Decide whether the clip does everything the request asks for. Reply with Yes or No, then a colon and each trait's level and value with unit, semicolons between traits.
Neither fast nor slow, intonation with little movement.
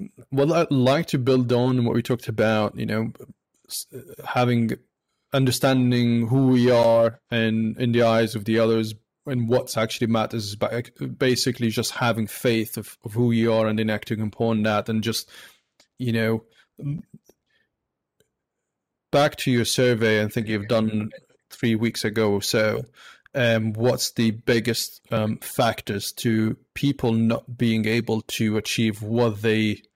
Yes: average, 150 wpm; narrow, 2.0 semitones